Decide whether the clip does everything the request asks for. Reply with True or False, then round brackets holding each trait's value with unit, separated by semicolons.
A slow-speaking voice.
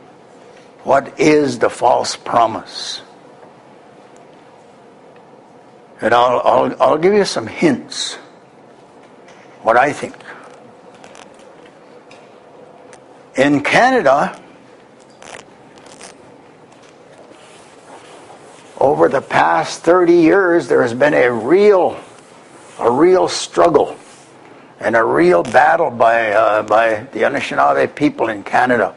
True (90 wpm)